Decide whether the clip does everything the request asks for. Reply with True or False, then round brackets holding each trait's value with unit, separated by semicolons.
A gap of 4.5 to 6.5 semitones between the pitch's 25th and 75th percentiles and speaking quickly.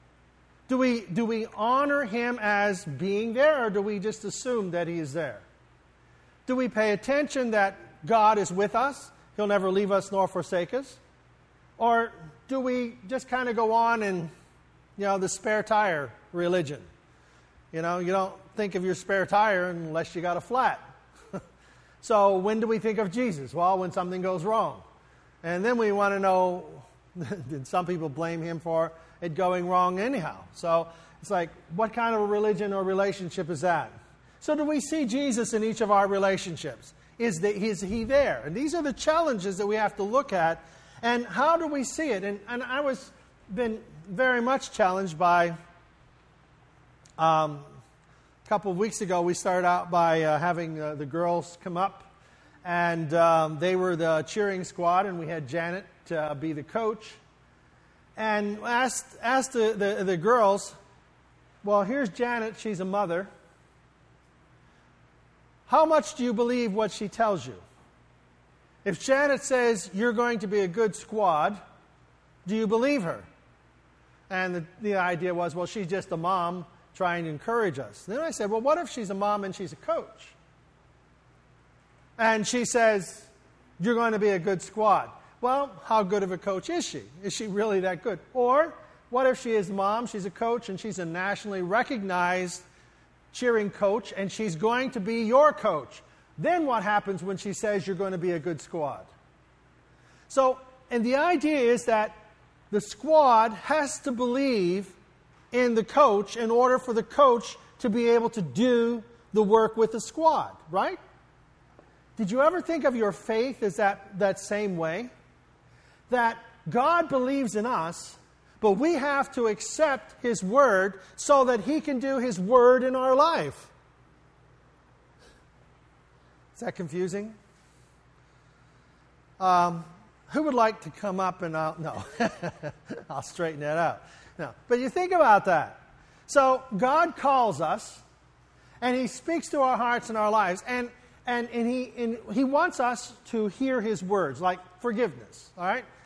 False (5.2 semitones; 170 wpm)